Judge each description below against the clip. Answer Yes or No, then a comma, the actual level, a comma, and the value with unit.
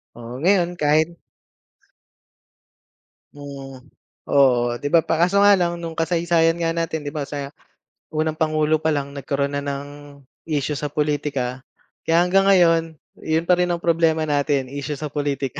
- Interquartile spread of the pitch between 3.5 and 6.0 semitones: No, average, 2.9 semitones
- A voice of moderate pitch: Yes, medium, 155 Hz